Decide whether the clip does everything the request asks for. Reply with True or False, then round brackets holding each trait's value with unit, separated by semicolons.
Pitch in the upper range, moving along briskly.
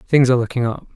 False (125 Hz; 250 wpm)